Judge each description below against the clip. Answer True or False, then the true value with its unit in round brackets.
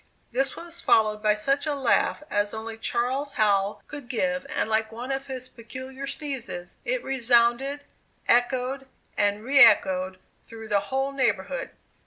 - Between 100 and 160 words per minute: True (150 wpm)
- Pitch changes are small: False (3.8 semitones)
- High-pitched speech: True (250 Hz)